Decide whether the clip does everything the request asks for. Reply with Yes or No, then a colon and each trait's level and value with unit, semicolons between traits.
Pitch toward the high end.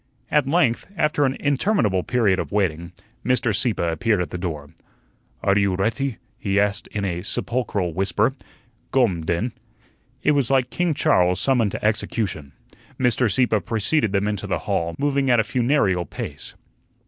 No: low, 105 Hz